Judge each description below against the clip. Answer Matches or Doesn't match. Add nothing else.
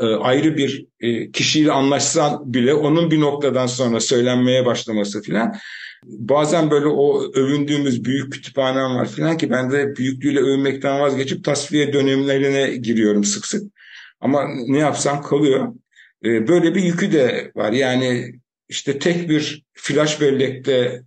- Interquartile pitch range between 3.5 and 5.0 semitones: Doesn't match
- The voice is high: Doesn't match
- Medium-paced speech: Matches